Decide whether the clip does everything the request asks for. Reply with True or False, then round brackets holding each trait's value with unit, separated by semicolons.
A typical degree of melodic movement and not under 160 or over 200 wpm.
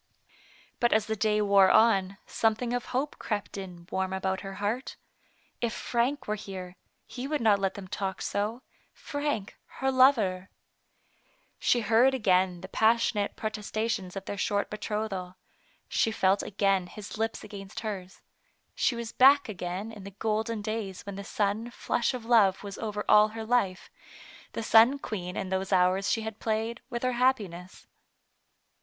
True (3.0 semitones; 165 wpm)